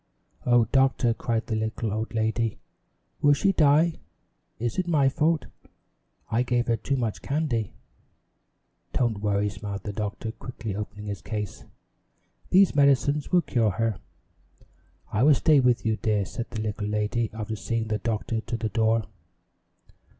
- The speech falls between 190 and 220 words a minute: No, average, 150 wpm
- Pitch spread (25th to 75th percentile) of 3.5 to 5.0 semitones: Yes, average, 3.8 semitones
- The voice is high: No, low, 115 Hz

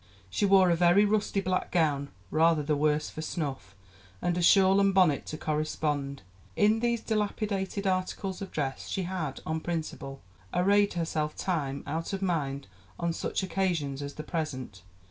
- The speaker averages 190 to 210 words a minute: No, average, 165 wpm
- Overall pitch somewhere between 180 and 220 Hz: No, medium, 170 Hz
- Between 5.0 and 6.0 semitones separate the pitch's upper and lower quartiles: No, average, 4.4 semitones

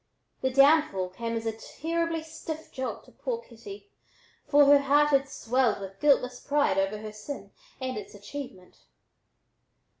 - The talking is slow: No, average, 150 wpm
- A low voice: No, very high, 270 Hz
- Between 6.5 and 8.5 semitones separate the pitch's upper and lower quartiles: No, wide, 5.6 semitones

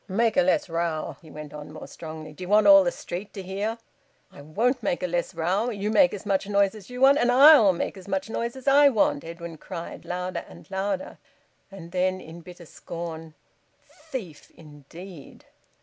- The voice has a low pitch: No, high, 190 Hz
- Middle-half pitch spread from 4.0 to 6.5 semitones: Yes, average, 4.6 semitones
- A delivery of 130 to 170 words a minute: No, average, 195 wpm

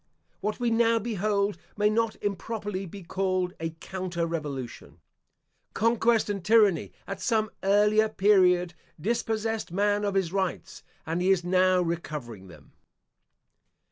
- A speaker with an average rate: No, slow, 130 wpm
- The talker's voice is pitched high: Yes, high, 195 Hz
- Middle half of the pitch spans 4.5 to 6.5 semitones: No, average, 3.4 semitones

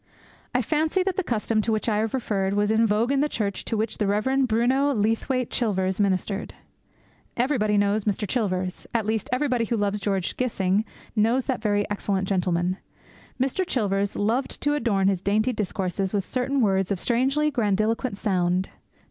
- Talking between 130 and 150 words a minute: No, average, 175 wpm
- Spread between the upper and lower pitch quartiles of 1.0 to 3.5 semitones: No, average, 4.0 semitones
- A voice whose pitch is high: Yes, high, 215 Hz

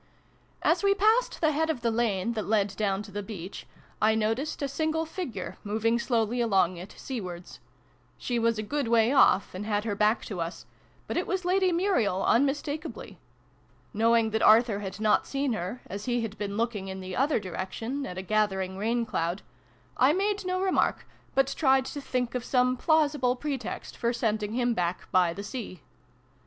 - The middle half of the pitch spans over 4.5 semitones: Yes, average, 5.1 semitones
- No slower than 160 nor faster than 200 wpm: Yes, average, 185 wpm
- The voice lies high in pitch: Yes, high, 230 Hz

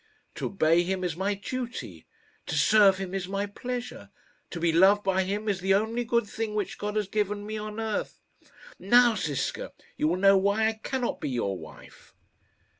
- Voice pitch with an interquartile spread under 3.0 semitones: Yes, narrow, 2.6 semitones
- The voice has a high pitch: Yes, high, 200 Hz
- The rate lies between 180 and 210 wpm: Yes, average, 190 wpm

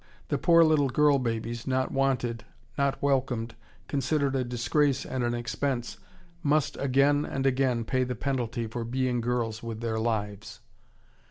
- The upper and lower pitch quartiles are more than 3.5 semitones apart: No, average, 2.8 semitones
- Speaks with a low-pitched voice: Yes, low, 130 Hz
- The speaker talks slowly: No, average, 150 wpm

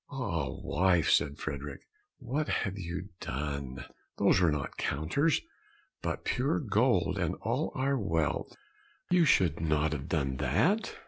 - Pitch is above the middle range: No, very low, 80 Hz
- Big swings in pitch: Yes, wide, 8.6 semitones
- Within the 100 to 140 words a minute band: Yes, slow, 135 wpm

